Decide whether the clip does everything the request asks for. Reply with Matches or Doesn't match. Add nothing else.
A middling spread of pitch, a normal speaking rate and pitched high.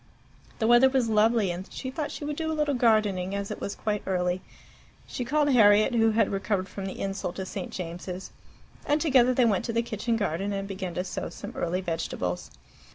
Doesn't match